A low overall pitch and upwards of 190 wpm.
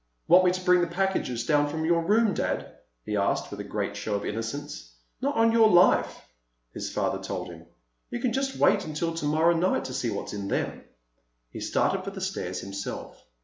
No: medium, 165 Hz; average, 200 wpm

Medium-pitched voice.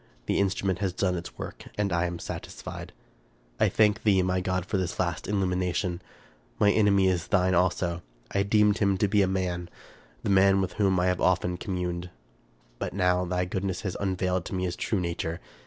No: very low, 95 Hz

